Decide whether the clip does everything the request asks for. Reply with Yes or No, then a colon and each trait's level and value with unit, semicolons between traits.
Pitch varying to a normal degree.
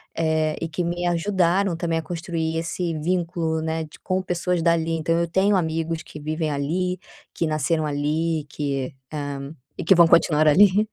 No: narrow, 2.0 semitones